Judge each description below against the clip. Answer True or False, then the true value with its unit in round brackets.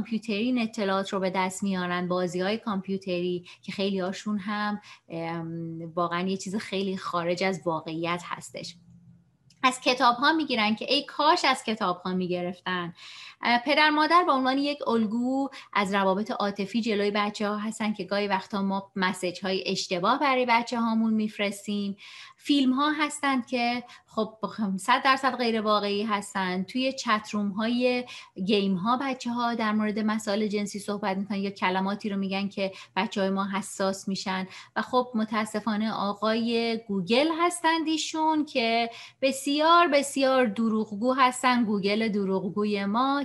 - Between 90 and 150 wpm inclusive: True (145 wpm)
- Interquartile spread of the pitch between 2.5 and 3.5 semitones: False (4.3 semitones)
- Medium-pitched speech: False (210 Hz)